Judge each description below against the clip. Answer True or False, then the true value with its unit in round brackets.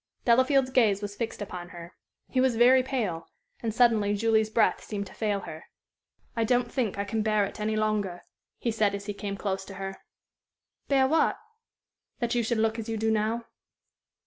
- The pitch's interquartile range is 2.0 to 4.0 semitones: True (2.8 semitones)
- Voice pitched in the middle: False (220 Hz)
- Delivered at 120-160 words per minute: False (190 wpm)